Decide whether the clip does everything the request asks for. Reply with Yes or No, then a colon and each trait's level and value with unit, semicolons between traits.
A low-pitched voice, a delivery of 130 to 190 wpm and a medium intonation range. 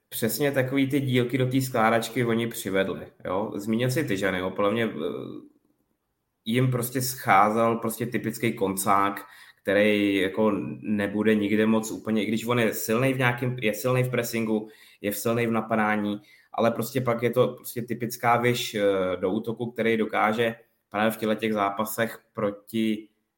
No: low, 115 Hz; average, 155 wpm; narrow, 2.1 semitones